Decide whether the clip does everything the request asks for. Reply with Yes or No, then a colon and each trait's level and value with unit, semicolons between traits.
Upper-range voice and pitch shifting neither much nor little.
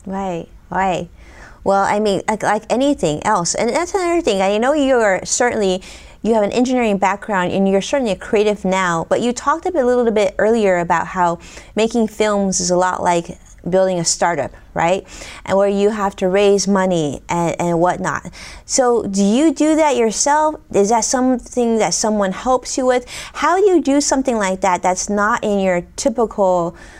Yes: high, 205 Hz; average, 4.7 semitones